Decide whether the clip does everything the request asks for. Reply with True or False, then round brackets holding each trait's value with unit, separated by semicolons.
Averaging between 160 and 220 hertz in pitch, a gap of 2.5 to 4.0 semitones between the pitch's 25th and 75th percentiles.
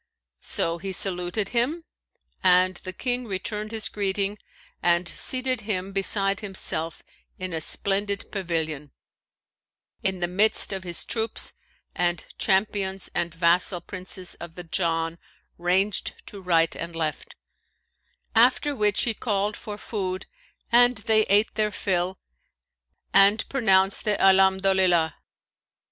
True (190 Hz; 2.9 semitones)